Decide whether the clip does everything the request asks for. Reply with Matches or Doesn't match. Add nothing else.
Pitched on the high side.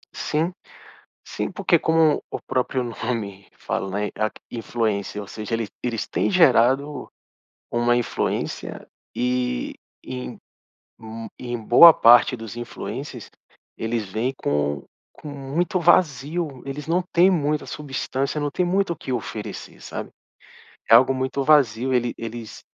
Doesn't match